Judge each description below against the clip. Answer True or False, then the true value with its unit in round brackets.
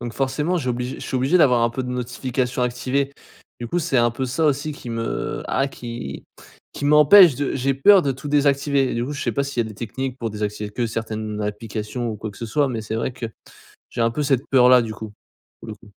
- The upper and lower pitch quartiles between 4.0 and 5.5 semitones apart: False (3.3 semitones)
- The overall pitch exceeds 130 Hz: False (125 Hz)